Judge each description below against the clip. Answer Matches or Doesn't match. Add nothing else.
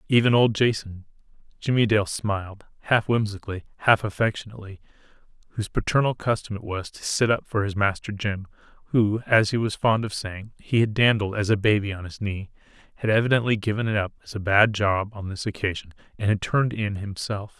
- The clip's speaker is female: Doesn't match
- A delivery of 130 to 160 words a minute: Doesn't match